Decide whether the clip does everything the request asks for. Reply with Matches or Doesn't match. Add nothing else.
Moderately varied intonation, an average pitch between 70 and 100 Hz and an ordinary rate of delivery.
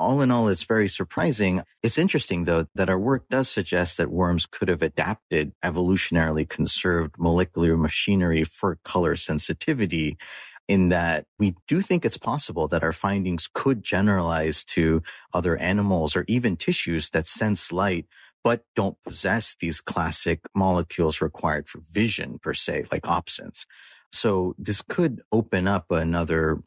Matches